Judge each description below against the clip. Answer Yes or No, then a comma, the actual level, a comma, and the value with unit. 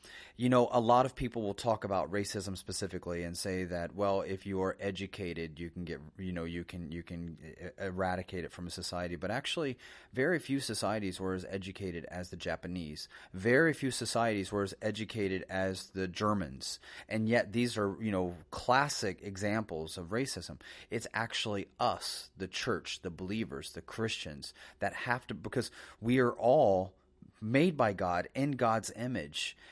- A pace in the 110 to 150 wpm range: No, average, 170 wpm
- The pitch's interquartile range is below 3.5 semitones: No, average, 3.8 semitones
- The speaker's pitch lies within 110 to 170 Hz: No, very low, 95 Hz